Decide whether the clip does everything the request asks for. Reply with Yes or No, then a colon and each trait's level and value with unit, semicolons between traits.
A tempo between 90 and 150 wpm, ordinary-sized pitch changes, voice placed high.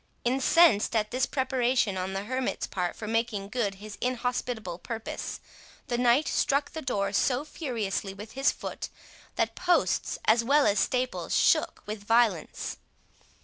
Yes: average, 145 wpm; average, 4.0 semitones; high, 235 Hz